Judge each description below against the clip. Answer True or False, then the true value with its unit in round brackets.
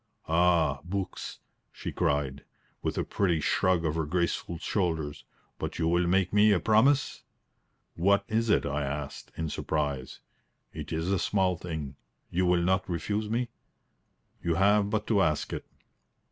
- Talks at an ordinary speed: True (155 wpm)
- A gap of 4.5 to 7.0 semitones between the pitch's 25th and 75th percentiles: False (4.0 semitones)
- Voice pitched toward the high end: False (90 Hz)